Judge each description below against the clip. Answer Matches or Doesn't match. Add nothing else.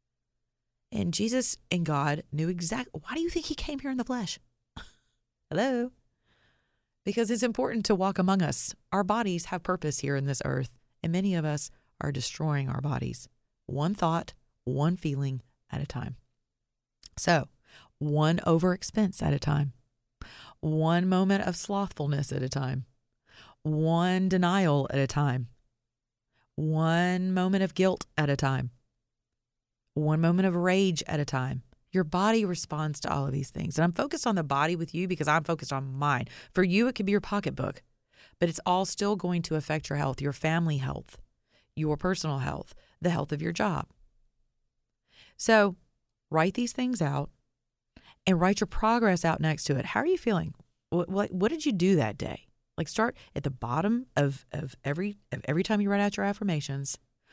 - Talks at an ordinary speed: Matches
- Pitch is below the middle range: Doesn't match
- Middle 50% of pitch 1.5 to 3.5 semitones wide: Doesn't match